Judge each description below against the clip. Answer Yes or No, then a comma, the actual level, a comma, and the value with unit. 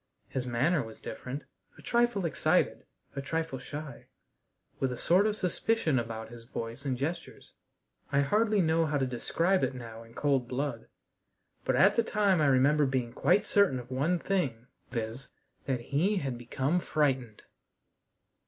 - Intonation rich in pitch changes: Yes, wide, 5.9 semitones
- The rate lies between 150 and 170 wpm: Yes, average, 160 wpm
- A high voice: No, medium, 140 Hz